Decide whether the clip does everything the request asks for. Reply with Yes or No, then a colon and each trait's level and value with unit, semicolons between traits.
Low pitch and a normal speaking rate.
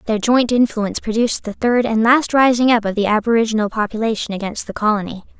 No: high, 225 Hz; average, 190 wpm